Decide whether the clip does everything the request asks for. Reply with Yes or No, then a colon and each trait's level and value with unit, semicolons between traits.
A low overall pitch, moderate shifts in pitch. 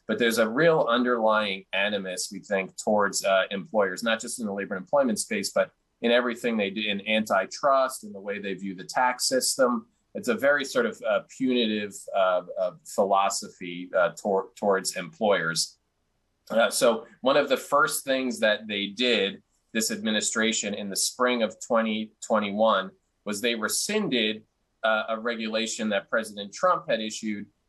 Yes: low, 110 Hz; average, 3.6 semitones